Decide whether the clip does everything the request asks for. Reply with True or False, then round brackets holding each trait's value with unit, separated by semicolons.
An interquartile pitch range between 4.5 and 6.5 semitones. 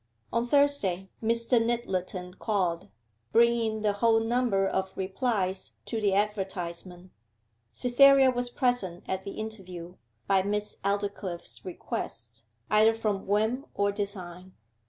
False (3.7 semitones)